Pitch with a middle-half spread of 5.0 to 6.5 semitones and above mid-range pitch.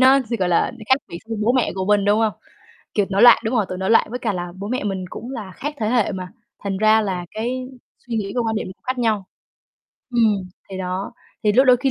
No: average, 4.0 semitones; high, 215 Hz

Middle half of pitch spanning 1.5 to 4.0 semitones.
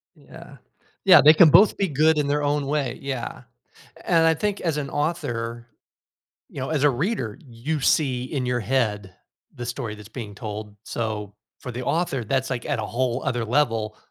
No: average, 4.4 semitones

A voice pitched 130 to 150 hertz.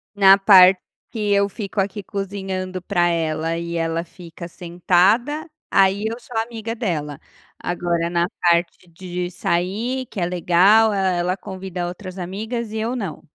No: medium, 185 Hz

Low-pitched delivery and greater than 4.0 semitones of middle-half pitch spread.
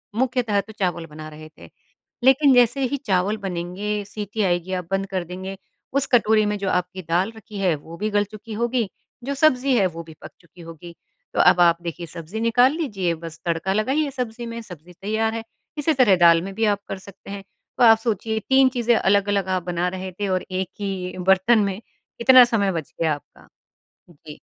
No: high, 200 Hz; average, 4.4 semitones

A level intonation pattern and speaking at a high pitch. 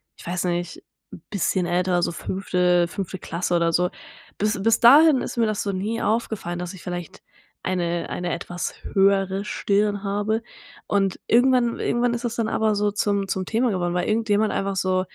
No: average, 3.6 semitones; high, 195 Hz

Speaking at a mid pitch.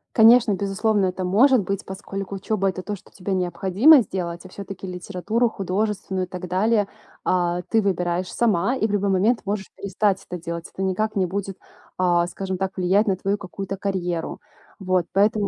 No: high, 195 Hz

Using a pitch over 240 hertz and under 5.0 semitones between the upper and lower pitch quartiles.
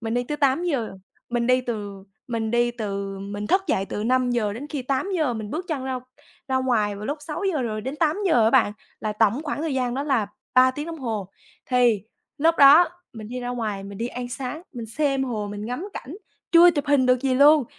Yes: very high, 250 Hz; average, 4.6 semitones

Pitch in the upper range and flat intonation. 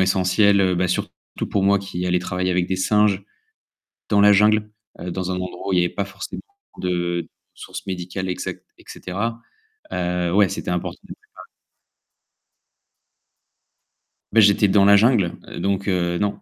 No: very low, 95 Hz; narrow, 2.1 semitones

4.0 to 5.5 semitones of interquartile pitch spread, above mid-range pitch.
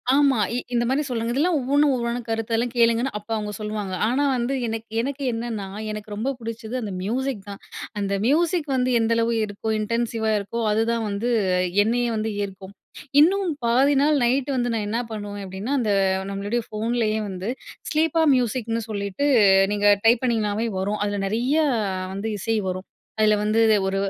No: average, 3.1 semitones; high, 230 Hz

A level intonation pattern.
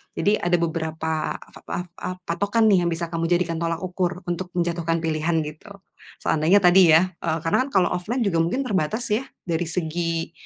Yes: narrow, 2.3 semitones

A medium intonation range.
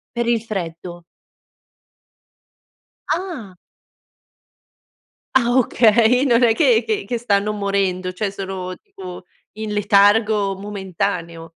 Yes: average, 3.5 semitones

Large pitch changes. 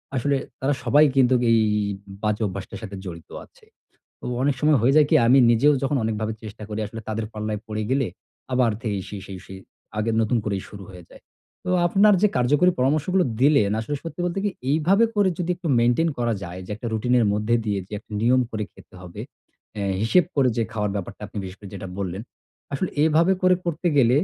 Yes: wide, 5.8 semitones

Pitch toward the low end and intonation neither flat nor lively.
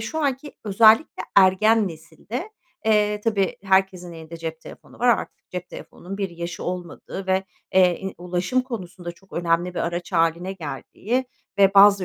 No: high, 190 Hz; average, 3.3 semitones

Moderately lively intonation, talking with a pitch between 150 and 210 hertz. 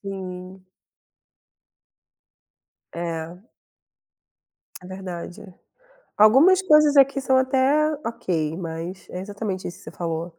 No: wide, 7.2 semitones; high, 190 Hz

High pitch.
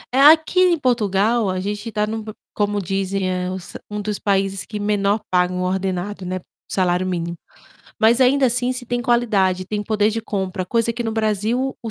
Yes: high, 210 Hz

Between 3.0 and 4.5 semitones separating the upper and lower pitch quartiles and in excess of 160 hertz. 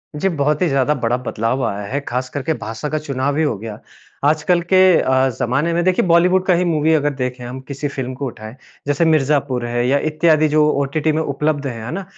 No: average, 3.6 semitones; medium, 145 Hz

